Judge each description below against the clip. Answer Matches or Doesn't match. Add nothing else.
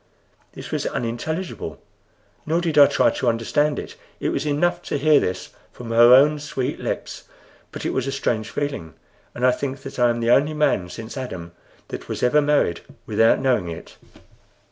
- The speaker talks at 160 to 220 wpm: Matches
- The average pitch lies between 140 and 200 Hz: Doesn't match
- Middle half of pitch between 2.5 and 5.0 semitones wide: Matches